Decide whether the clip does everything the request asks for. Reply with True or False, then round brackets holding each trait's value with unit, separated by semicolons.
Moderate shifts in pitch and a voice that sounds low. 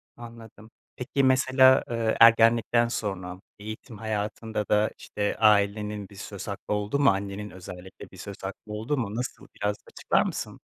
False (2.3 semitones; 110 Hz)